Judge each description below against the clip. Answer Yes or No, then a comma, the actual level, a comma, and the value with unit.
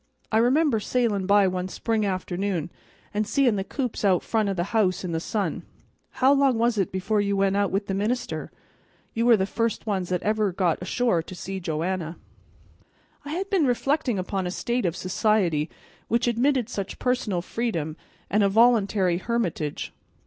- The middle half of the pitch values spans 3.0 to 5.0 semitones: Yes, average, 4.2 semitones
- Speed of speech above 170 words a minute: Yes, average, 180 wpm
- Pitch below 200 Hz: No, high, 205 Hz